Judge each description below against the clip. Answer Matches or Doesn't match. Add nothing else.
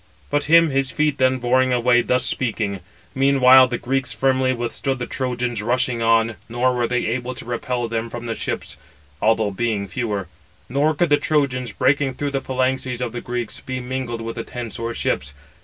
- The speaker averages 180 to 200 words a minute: Matches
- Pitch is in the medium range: Doesn't match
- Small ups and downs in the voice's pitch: Matches